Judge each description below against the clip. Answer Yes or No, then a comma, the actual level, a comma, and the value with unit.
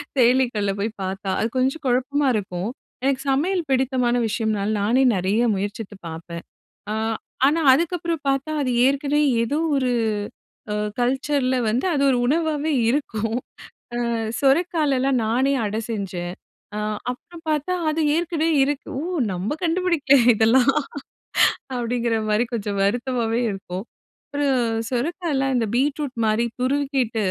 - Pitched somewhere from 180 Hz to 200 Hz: No, very high, 255 Hz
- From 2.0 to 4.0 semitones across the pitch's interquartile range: No, average, 4.6 semitones